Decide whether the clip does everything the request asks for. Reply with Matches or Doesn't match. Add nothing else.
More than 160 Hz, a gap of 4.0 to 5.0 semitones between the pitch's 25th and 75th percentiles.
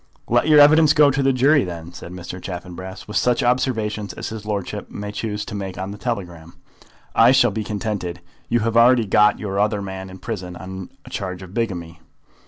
Doesn't match